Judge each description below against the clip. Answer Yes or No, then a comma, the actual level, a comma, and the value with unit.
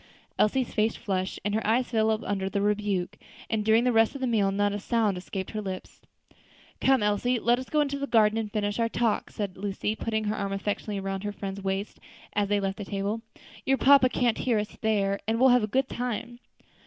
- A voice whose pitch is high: Yes, high, 210 Hz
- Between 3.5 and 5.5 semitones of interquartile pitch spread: No, average, 2.8 semitones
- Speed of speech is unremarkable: No, fast, 220 wpm